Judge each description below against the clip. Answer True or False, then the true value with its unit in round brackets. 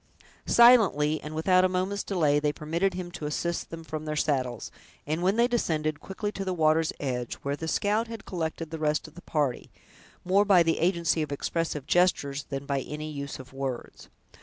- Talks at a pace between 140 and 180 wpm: False (195 wpm)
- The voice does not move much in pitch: False (3.7 semitones)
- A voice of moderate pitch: True (160 Hz)